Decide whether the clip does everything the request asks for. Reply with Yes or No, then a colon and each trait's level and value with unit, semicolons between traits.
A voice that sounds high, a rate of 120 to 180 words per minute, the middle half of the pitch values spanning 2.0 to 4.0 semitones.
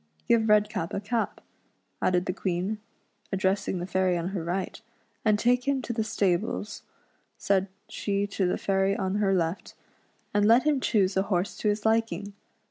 Yes: high, 200 Hz; average, 175 wpm; narrow, 2.4 semitones